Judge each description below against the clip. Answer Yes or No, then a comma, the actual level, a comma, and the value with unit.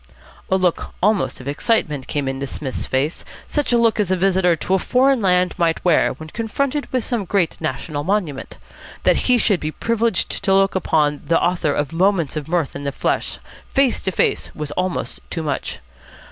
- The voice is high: No, medium, 180 Hz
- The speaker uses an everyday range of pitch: No, wide, 5.7 semitones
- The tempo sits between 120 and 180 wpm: No, average, 195 wpm